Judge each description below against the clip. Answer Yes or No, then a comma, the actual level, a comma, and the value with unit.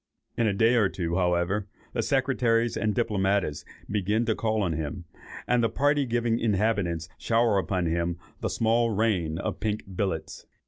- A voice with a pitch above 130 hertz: No, low, 105 Hz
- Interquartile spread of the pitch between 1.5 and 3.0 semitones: No, average, 4.2 semitones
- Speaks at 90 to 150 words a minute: No, average, 165 wpm